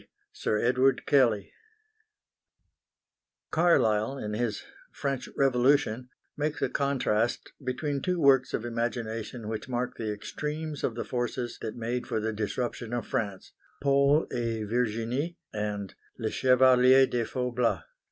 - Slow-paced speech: Yes, slow, 125 wpm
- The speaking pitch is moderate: No, low, 125 Hz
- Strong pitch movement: No, average, 3.3 semitones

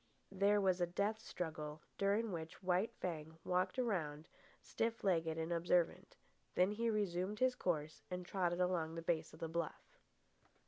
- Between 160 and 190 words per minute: Yes, average, 165 wpm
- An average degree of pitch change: Yes, average, 3.6 semitones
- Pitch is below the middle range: No, medium, 180 Hz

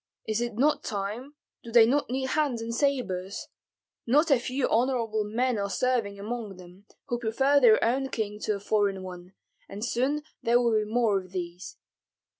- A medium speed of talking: Yes, average, 180 wpm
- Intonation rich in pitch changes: No, average, 4.0 semitones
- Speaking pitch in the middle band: No, high, 230 Hz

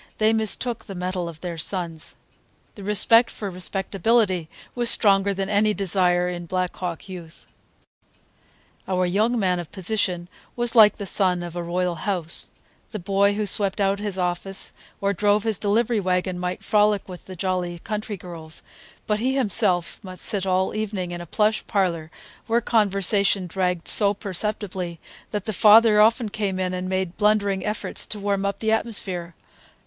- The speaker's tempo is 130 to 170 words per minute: Yes, average, 165 wpm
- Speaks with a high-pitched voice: Yes, high, 195 Hz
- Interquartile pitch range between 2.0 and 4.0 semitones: Yes, average, 2.7 semitones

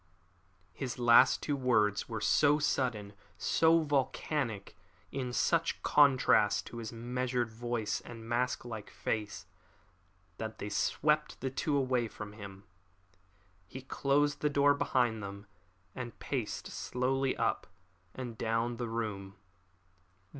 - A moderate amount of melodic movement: Yes, average, 3.5 semitones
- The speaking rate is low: Yes, slow, 125 wpm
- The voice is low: Yes, low, 120 Hz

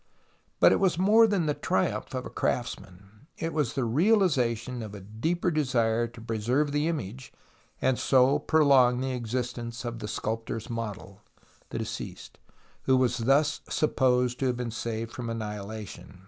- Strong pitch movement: No, average, 4.2 semitones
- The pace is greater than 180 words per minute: No, average, 165 wpm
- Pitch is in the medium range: No, low, 125 Hz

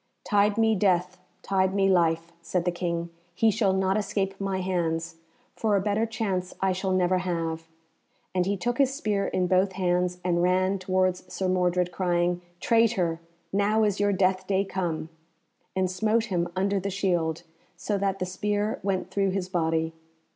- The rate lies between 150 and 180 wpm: Yes, average, 170 wpm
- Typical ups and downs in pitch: No, narrow, 2.0 semitones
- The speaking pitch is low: No, medium, 185 Hz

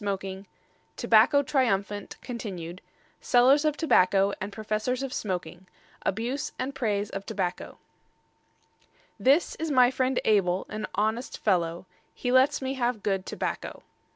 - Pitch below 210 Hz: No, high, 215 Hz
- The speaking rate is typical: No, slow, 125 wpm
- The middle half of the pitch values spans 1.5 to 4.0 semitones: No, average, 5.0 semitones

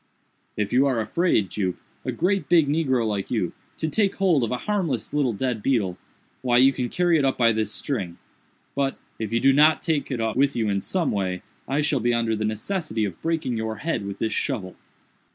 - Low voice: Yes, low, 125 Hz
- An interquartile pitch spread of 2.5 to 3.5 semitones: No, wide, 5.5 semitones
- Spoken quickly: Yes, fast, 210 wpm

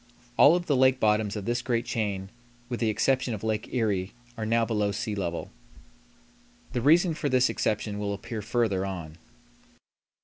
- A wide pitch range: No, average, 3.6 semitones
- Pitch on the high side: No, low, 110 Hz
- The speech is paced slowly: No, average, 170 wpm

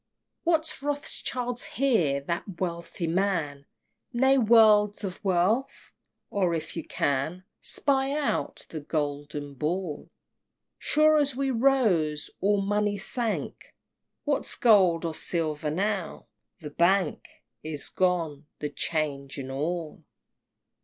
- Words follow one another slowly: Yes, slow, 115 wpm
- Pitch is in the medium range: Yes, medium, 180 Hz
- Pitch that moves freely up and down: Yes, wide, 6.9 semitones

